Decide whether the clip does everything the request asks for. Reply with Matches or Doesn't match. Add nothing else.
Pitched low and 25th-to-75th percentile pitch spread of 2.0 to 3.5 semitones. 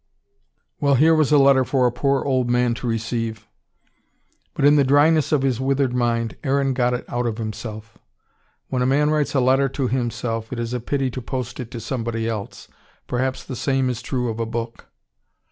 Matches